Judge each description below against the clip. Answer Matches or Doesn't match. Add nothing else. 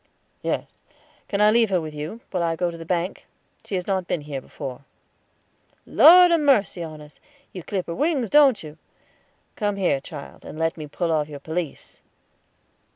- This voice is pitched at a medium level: Matches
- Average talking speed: Matches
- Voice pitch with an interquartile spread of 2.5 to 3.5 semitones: Doesn't match